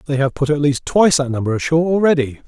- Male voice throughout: Yes, male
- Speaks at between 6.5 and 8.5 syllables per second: Yes, 7.1 syllables/s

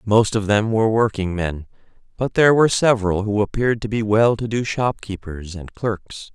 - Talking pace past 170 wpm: Yes, average, 190 wpm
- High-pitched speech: No, low, 110 Hz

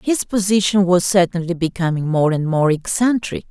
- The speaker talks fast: No, average, 155 wpm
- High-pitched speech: No, medium, 180 Hz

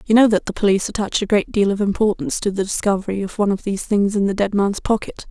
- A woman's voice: Yes, female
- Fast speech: Yes, fast, 270 wpm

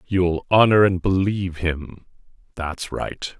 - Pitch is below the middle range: Yes, very low, 90 Hz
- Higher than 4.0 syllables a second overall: No, 3.7 syllables/s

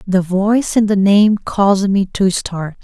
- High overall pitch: Yes, high, 195 Hz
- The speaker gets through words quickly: No, average, 190 wpm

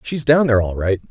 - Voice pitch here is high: No, low, 120 Hz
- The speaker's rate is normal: No, fast, 270 wpm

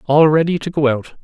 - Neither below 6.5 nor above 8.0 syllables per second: No, 5.6 syllables/s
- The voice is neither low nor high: Yes, medium, 150 Hz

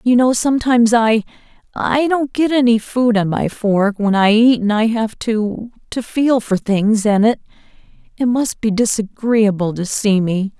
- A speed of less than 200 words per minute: Yes, average, 165 wpm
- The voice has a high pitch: Yes, high, 225 Hz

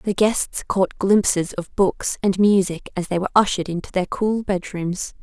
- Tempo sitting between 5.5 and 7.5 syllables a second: No, 4.6 syllables/s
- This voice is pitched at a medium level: No, high, 195 Hz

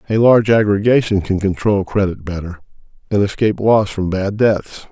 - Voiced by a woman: No, male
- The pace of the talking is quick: No, average, 160 wpm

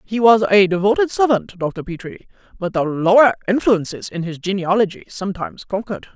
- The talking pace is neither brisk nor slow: Yes, average, 155 wpm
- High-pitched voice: Yes, high, 200 Hz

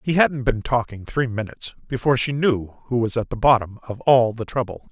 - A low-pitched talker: Yes, low, 120 Hz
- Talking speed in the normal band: No, fast, 220 wpm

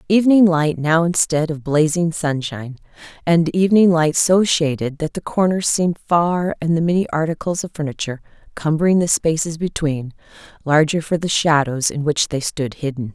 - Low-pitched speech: No, medium, 160 Hz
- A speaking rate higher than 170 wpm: No, average, 165 wpm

